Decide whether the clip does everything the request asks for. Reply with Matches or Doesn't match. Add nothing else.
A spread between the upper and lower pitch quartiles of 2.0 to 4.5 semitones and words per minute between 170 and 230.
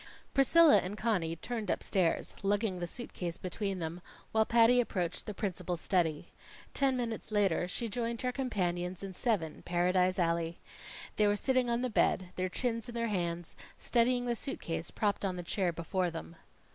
Doesn't match